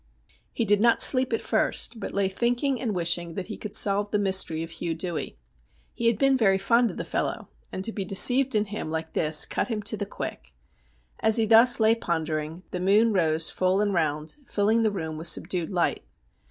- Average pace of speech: No, fast, 210 wpm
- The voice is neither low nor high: No, high, 200 Hz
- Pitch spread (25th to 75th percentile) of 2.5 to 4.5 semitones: No, average, 4.9 semitones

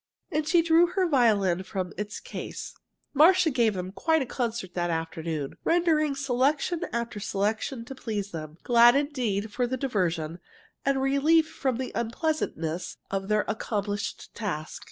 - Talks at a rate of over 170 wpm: No, average, 150 wpm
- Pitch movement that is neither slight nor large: No, wide, 6.6 semitones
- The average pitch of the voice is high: Yes, high, 235 Hz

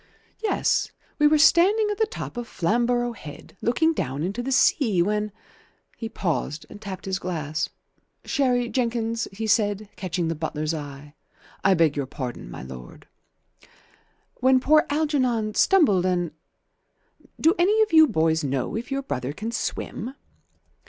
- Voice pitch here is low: No, high, 215 Hz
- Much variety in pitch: Yes, wide, 8.4 semitones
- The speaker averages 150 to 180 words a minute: Yes, average, 155 wpm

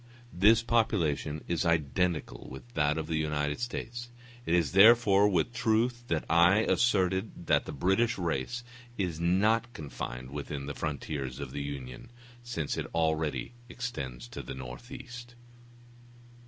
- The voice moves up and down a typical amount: No, wide, 7.7 semitones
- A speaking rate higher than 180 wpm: No, average, 140 wpm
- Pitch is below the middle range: Yes, very low, 85 Hz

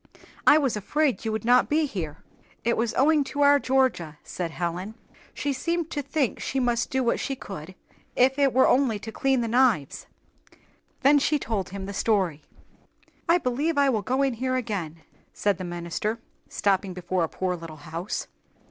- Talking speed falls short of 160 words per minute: No, average, 185 wpm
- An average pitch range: No, wide, 6.6 semitones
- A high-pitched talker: Yes, high, 230 Hz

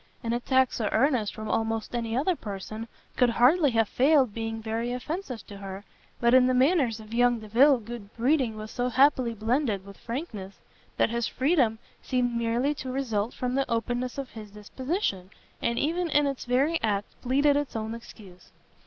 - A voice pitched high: Yes, high, 240 Hz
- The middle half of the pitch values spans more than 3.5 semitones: No, average, 3.2 semitones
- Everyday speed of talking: Yes, average, 180 wpm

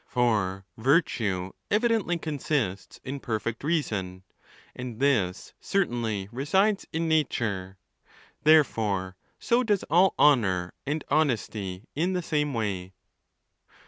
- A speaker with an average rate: No, slow, 110 wpm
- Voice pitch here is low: Yes, low, 125 Hz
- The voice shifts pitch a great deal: Yes, wide, 8.3 semitones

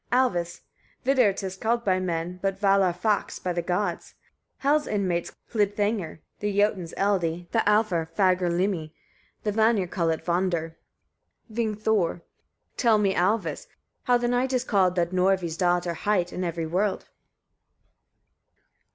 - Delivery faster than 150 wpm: No, average, 145 wpm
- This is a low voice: No, high, 190 Hz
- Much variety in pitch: No, average, 3.4 semitones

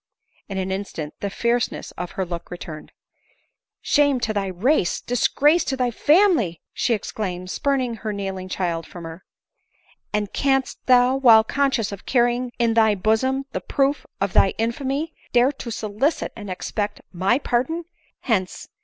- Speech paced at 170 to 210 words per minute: Yes, average, 175 wpm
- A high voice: Yes, high, 225 Hz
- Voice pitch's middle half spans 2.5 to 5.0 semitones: No, wide, 5.6 semitones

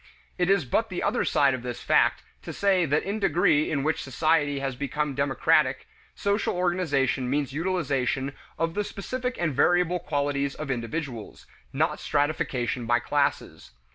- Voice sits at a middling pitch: Yes, medium, 145 Hz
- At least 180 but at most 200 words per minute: No, average, 160 wpm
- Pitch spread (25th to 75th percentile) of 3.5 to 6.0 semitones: Yes, average, 4.6 semitones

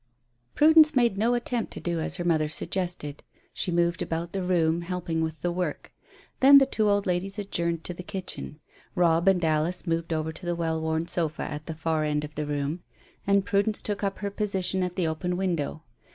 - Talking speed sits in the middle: No, fast, 210 wpm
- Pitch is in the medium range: Yes, medium, 175 Hz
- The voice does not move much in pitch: No, average, 3.4 semitones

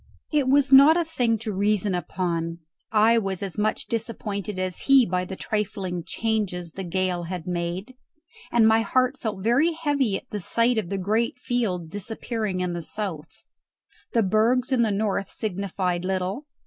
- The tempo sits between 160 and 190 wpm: Yes, average, 170 wpm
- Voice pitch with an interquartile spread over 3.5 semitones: Yes, average, 4.2 semitones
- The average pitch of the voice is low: No, high, 210 Hz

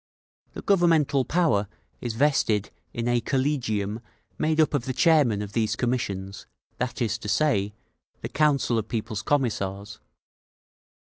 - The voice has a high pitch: No, low, 120 Hz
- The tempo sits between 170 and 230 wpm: No, slow, 135 wpm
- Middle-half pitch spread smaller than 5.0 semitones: No, wide, 5.6 semitones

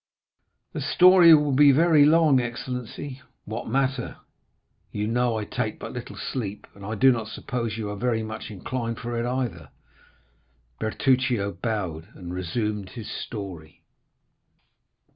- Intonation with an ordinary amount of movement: Yes, average, 3.8 semitones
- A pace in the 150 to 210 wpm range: No, average, 140 wpm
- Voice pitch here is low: Yes, low, 115 Hz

